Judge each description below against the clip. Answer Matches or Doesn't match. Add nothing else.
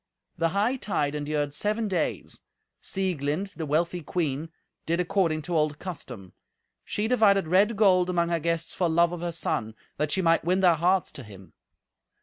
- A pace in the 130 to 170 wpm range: Matches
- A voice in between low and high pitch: Matches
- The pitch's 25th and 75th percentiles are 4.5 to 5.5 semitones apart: Doesn't match